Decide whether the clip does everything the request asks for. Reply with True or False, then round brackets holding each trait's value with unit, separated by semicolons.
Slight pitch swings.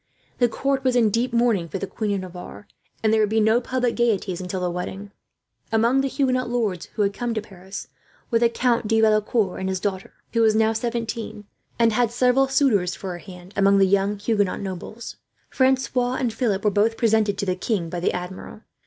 False (3.6 semitones)